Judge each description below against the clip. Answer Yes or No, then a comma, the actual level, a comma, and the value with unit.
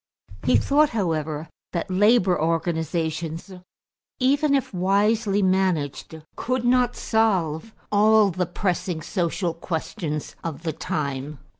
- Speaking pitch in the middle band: Yes, medium, 180 Hz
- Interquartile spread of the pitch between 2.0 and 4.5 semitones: No, average, 5.1 semitones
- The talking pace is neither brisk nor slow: No, slow, 110 wpm